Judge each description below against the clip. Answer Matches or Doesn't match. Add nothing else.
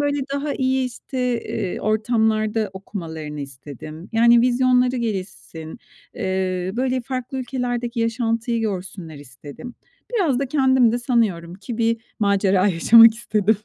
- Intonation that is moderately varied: Matches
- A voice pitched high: Matches